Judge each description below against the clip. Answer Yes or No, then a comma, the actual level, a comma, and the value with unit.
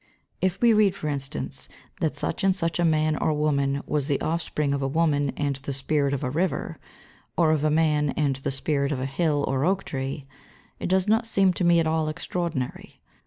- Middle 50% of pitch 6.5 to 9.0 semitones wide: No, average, 3.5 semitones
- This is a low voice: No, medium, 155 Hz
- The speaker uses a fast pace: Yes, fast, 215 wpm